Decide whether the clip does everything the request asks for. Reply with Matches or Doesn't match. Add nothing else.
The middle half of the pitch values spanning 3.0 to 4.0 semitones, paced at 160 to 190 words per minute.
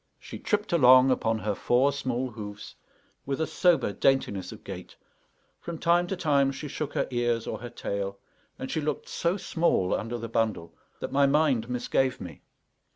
Doesn't match